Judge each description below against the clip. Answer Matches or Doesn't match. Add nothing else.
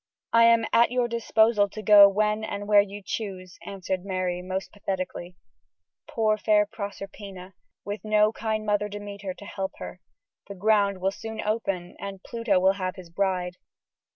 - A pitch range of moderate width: Doesn't match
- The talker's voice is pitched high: Matches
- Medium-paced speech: Matches